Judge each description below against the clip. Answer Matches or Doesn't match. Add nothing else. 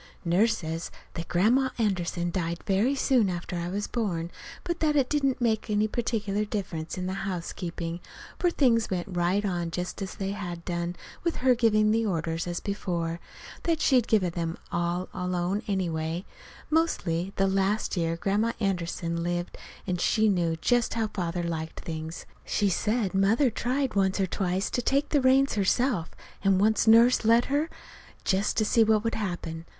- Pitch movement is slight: Doesn't match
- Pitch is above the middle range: Matches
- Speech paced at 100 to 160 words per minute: Doesn't match